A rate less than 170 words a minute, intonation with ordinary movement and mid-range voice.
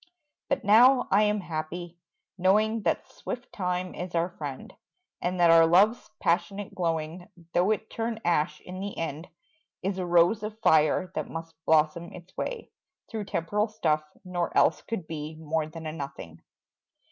Yes: average, 160 wpm; average, 4.1 semitones; medium, 175 Hz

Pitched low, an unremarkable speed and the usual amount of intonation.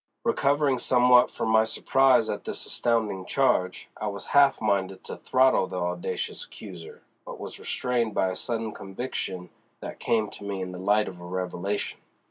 Yes: low, 105 Hz; average, 170 wpm; average, 4.9 semitones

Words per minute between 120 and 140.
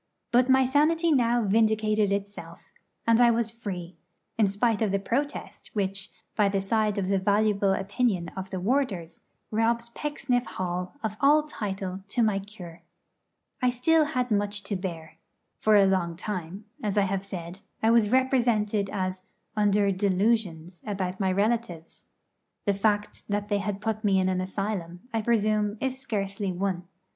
No: average, 160 wpm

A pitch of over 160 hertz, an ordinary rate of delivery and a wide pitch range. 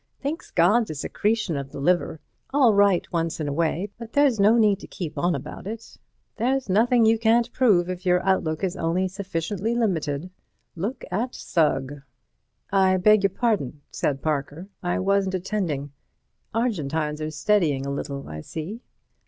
Yes: medium, 185 Hz; average, 160 wpm; wide, 5.7 semitones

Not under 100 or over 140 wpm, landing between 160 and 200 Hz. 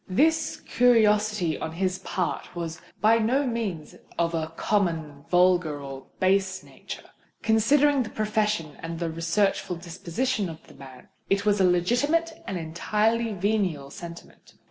Yes: slow, 135 wpm; high, 190 Hz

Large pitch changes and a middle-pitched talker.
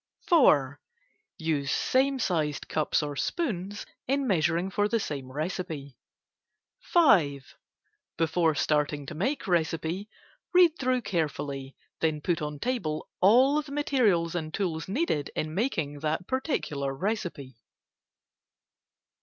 Yes: wide, 7.5 semitones; medium, 165 Hz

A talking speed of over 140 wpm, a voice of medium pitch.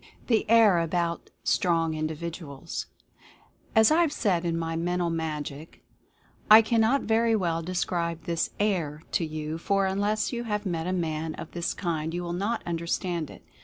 Yes: average, 165 wpm; medium, 170 Hz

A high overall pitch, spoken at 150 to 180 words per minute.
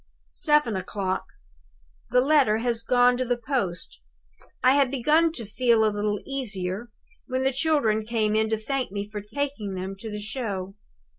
Yes: high, 230 Hz; average, 165 wpm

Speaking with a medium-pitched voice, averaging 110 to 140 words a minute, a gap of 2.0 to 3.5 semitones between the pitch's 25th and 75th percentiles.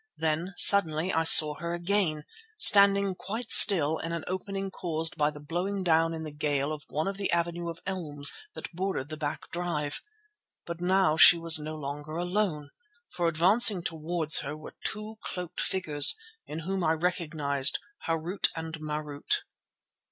No: medium, 165 Hz; average, 160 wpm; average, 3.2 semitones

